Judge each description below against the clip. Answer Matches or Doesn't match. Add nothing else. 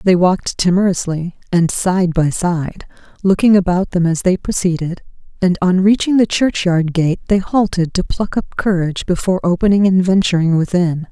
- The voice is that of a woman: Matches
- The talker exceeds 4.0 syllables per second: Matches